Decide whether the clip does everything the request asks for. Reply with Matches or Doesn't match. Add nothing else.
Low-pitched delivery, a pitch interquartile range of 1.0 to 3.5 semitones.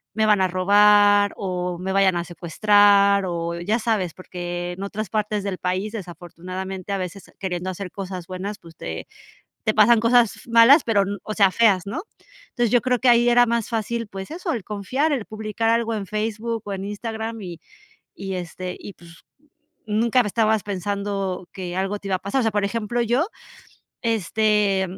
Doesn't match